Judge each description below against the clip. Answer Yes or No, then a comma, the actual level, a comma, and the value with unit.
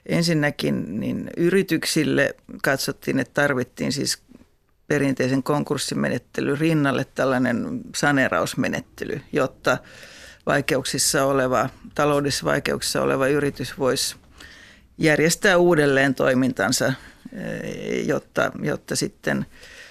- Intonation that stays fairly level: No, average, 3.0 semitones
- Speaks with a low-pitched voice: No, medium, 145 Hz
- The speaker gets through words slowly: Yes, slow, 75 wpm